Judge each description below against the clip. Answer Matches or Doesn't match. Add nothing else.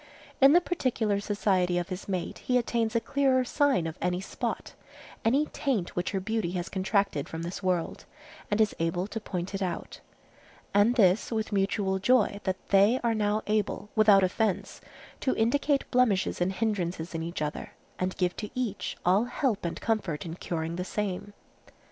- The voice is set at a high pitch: Matches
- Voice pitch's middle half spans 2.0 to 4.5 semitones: Matches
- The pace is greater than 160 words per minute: Matches